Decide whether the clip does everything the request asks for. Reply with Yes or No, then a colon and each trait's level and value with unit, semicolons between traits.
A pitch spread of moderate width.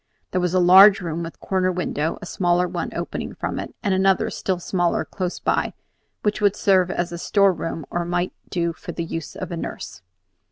No: narrow, 1.8 semitones